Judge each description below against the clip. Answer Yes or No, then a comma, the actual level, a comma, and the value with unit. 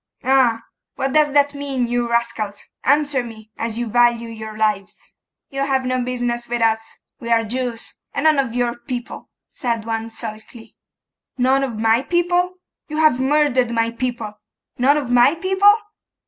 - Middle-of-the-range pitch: No, high, 245 Hz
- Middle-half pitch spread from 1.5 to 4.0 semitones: Yes, average, 3.2 semitones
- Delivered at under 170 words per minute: Yes, average, 160 wpm